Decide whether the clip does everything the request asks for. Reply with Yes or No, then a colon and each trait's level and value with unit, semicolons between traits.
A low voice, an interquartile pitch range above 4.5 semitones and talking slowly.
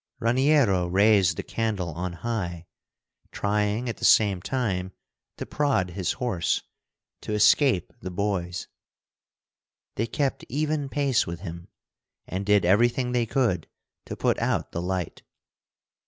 Yes: low, 105 Hz; average, 5.2 semitones; slow, 130 wpm